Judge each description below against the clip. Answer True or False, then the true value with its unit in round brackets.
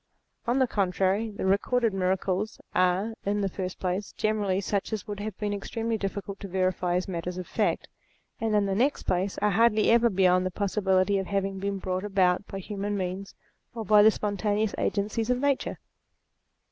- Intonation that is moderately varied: False (2.3 semitones)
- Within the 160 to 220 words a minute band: True (185 wpm)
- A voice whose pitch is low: False (200 Hz)